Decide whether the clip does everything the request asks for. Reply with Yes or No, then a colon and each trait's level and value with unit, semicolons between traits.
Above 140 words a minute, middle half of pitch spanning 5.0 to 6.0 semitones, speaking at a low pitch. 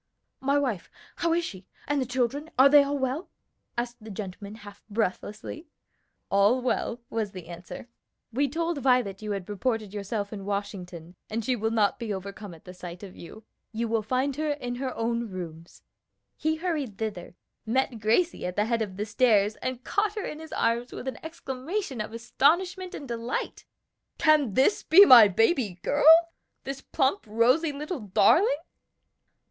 No: average, 170 wpm; wide, 5.6 semitones; high, 235 Hz